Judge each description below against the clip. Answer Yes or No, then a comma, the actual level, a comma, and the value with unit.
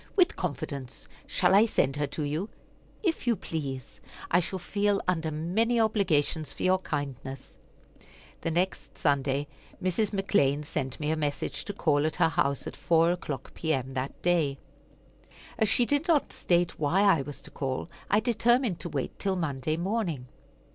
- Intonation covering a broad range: Yes, wide, 5.8 semitones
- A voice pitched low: No, medium, 165 Hz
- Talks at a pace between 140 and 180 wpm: Yes, average, 165 wpm